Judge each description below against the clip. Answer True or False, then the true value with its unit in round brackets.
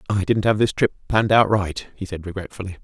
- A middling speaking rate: False (235 wpm)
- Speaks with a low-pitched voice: True (100 Hz)